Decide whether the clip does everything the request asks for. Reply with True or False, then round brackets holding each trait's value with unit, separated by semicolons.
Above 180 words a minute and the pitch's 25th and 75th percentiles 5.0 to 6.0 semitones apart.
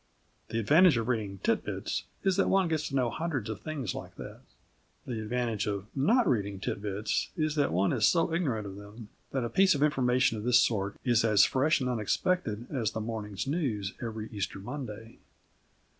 True (195 wpm; 5.6 semitones)